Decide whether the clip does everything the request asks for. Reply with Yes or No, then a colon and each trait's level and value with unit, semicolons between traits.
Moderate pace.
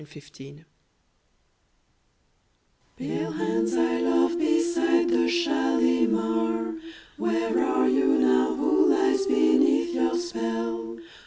No: slow, 95 wpm